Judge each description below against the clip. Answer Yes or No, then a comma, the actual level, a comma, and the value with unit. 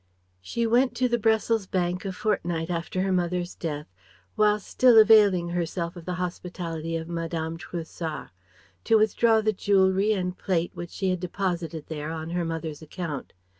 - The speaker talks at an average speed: Yes, average, 165 wpm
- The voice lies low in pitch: No, medium, 180 Hz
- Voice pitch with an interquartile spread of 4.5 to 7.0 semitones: No, average, 3.6 semitones